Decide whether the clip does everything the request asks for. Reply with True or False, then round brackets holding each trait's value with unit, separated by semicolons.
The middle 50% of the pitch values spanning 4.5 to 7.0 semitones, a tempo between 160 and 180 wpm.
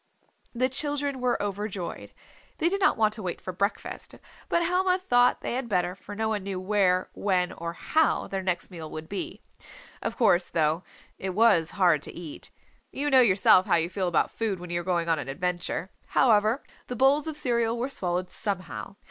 False (5.5 semitones; 195 wpm)